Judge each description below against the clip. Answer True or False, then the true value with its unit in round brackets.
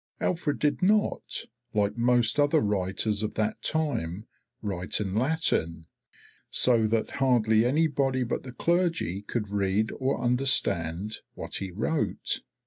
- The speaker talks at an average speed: False (130 wpm)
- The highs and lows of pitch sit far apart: True (5.7 semitones)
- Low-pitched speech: True (115 Hz)